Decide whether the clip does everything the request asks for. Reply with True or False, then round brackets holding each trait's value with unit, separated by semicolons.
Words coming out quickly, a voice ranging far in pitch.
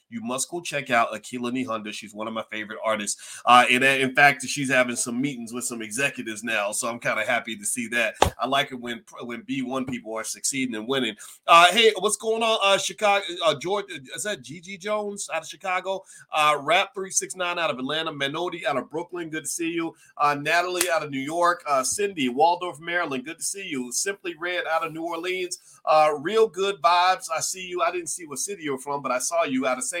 True (235 wpm; 6.4 semitones)